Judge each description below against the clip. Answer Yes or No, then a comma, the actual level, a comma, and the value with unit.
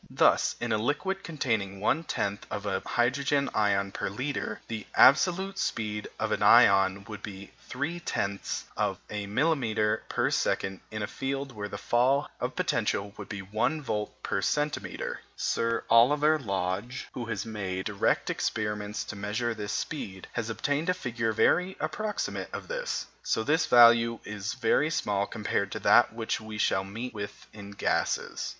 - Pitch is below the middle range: Yes, low, 110 Hz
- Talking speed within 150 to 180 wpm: Yes, average, 155 wpm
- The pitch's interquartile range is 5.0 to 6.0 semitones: Yes, average, 5.3 semitones